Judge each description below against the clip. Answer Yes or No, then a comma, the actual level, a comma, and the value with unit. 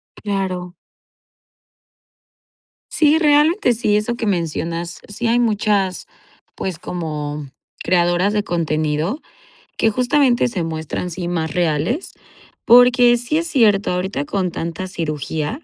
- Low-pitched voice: No, high, 190 Hz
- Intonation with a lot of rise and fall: Yes, wide, 6.2 semitones